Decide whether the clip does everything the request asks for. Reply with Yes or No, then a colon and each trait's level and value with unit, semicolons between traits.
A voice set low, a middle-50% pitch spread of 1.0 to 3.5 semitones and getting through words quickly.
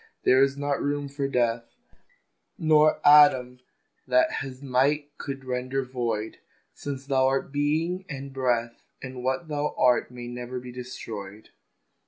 No: low, 130 Hz; narrow, 2.4 semitones; average, 140 wpm